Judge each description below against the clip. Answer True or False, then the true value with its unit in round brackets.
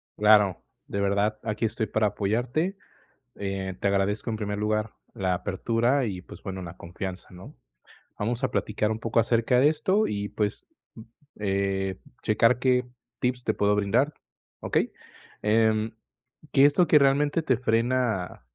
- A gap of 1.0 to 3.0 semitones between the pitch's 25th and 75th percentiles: False (3.7 semitones)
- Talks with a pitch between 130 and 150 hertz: False (110 Hz)